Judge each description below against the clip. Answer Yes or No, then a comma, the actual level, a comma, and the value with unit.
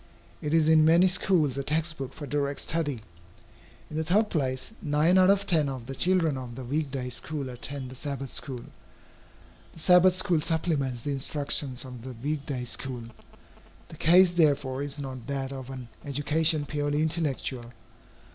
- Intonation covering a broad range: No, average, 3.4 semitones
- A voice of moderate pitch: Yes, medium, 145 Hz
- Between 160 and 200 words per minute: Yes, average, 175 wpm